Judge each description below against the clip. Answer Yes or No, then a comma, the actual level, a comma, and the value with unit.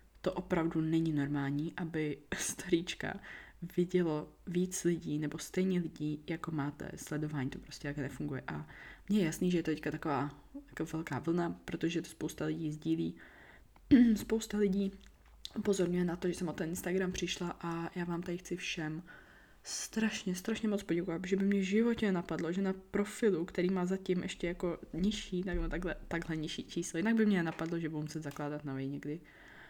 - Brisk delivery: Yes, fast, 175 wpm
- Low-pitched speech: No, medium, 170 Hz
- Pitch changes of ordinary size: Yes, average, 3.1 semitones